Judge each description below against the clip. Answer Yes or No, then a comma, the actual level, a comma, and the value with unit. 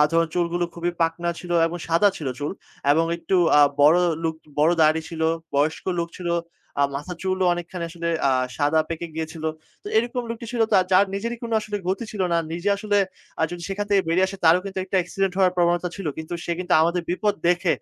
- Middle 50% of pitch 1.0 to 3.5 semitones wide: Yes, average, 2.7 semitones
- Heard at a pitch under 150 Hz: No, medium, 175 Hz